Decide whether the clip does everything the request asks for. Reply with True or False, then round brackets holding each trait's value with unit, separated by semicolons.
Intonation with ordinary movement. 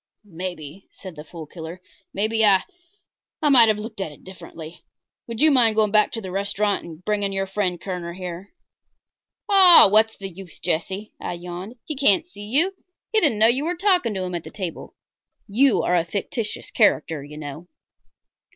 True (4.1 semitones)